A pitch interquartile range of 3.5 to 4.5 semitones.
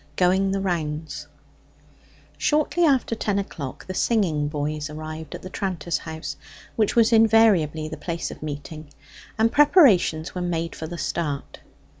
No: average, 5.2 semitones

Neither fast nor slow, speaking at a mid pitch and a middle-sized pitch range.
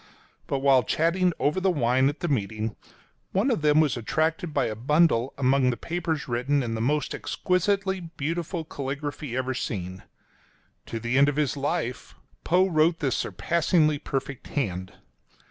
Yes: average, 165 wpm; medium, 145 Hz; average, 4.7 semitones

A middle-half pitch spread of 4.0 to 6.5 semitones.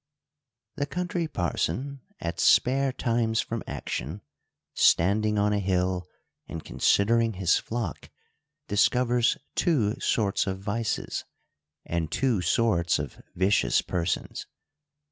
Yes: average, 4.7 semitones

